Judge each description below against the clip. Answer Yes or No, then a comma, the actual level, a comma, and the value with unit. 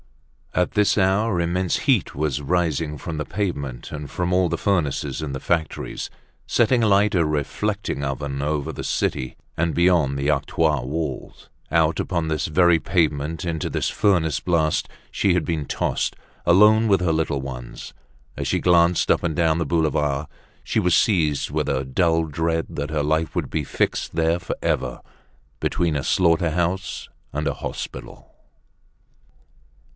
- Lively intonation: No, average, 3.2 semitones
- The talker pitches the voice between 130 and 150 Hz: No, very low, 80 Hz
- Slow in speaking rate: No, average, 160 wpm